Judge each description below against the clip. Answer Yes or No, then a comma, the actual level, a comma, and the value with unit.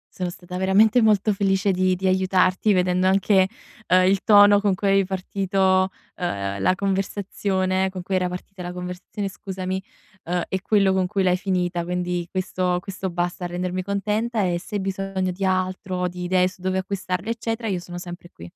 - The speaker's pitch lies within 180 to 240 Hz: Yes, medium, 185 Hz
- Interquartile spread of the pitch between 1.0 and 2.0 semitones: Yes, narrow, 1.4 semitones